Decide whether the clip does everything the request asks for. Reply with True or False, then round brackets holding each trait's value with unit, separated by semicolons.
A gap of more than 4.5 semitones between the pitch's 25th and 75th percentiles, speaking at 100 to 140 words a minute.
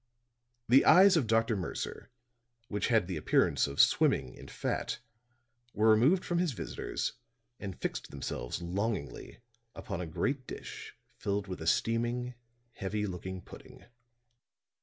True (5.3 semitones; 135 wpm)